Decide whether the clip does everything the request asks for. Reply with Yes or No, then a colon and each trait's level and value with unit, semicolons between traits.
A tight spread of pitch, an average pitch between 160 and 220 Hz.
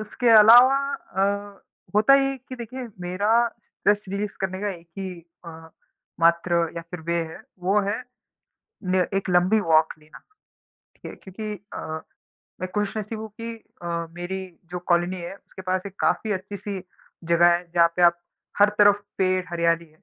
No: average, 3.4 semitones; high, 190 Hz